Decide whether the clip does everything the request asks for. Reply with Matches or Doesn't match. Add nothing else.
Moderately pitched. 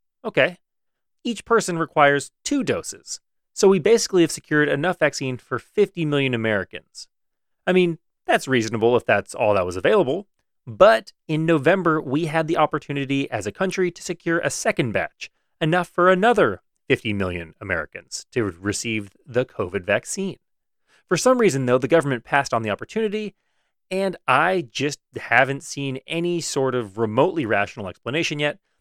Matches